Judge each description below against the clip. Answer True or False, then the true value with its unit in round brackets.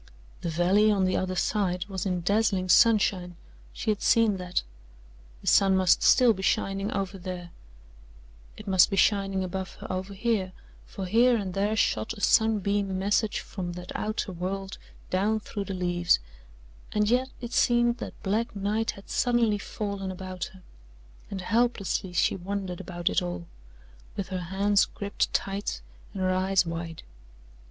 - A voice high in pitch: True (195 Hz)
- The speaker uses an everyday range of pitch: False (2.3 semitones)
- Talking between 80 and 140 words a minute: False (160 wpm)